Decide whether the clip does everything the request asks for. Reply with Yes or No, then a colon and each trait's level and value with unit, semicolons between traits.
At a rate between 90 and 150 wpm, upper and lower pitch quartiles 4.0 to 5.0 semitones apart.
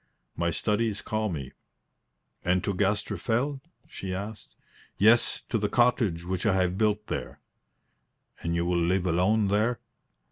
No: average, 145 wpm; average, 3.4 semitones